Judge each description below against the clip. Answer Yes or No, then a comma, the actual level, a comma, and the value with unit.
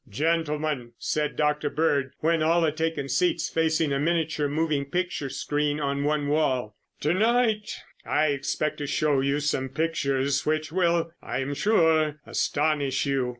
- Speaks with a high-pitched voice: No, medium, 150 Hz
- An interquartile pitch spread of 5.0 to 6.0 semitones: No, narrow, 2.5 semitones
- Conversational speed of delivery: Yes, average, 150 wpm